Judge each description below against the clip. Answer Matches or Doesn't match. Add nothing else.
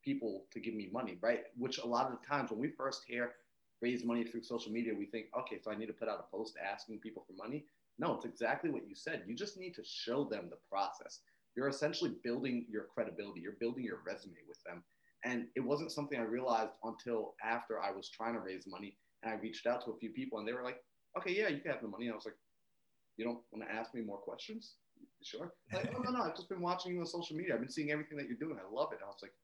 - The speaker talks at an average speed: Doesn't match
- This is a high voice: Doesn't match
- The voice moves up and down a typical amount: Doesn't match